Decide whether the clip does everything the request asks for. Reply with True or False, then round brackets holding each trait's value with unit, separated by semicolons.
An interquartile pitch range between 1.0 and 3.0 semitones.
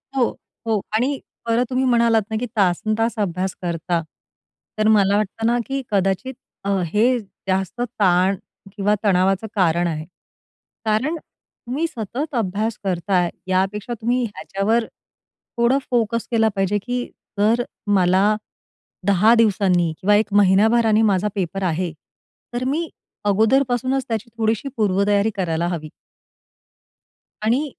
False (3.8 semitones)